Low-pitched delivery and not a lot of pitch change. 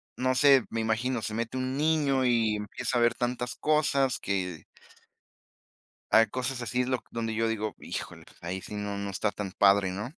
No: low, 115 Hz; average, 3.7 semitones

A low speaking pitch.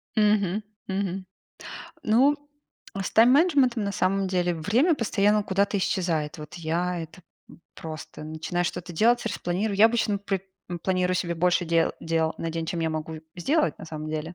No: medium, 185 Hz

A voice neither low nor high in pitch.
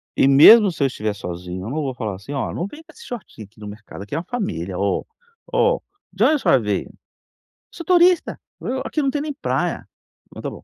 Yes: medium, 145 Hz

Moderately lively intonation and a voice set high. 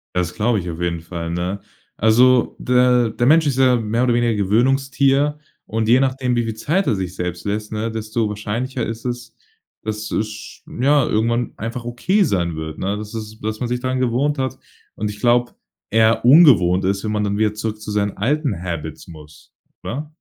No: average, 3.5 semitones; low, 110 Hz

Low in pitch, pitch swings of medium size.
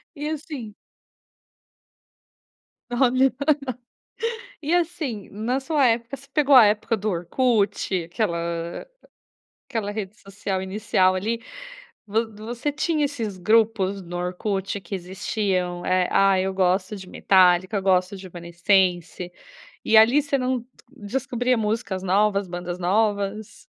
No: high, 205 Hz; average, 4.3 semitones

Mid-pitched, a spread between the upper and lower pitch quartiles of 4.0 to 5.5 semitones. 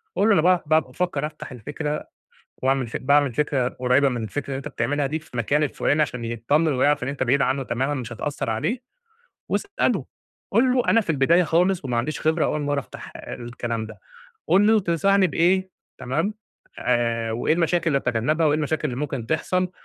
Yes: medium, 145 Hz; average, 4.8 semitones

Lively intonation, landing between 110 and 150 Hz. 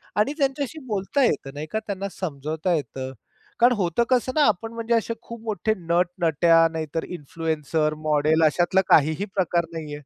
No: wide, 5.8 semitones; medium, 175 Hz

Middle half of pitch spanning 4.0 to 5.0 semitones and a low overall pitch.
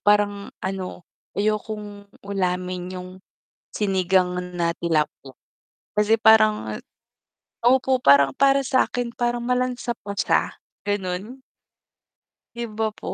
No: average, 4.5 semitones; high, 205 Hz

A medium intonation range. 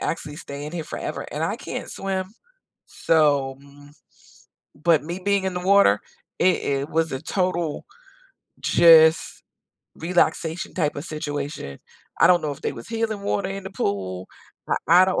Yes: average, 4.3 semitones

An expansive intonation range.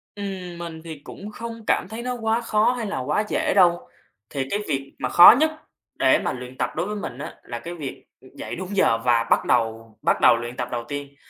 Yes: wide, 8.5 semitones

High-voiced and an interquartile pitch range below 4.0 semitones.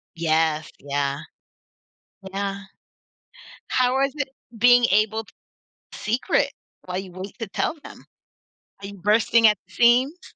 No: high, 210 Hz; average, 4.8 semitones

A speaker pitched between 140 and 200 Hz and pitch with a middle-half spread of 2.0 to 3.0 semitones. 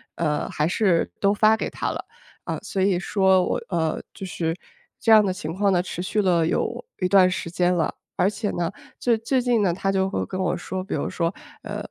Yes: medium, 185 Hz; narrow, 2.5 semitones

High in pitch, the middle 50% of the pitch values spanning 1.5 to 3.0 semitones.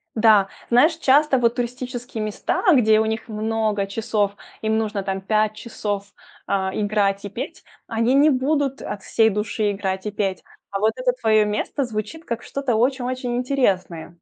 No: high, 220 Hz; average, 3.4 semitones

